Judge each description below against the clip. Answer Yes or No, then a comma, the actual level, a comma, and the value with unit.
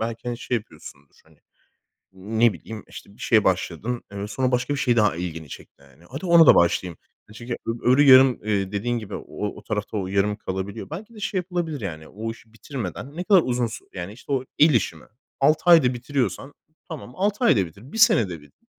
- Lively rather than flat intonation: Yes, wide, 5.9 semitones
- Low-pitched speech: Yes, low, 115 Hz